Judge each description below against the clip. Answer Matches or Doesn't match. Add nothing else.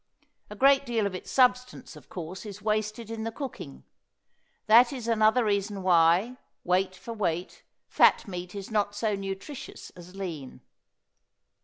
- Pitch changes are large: Doesn't match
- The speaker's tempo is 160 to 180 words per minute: Doesn't match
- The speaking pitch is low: Doesn't match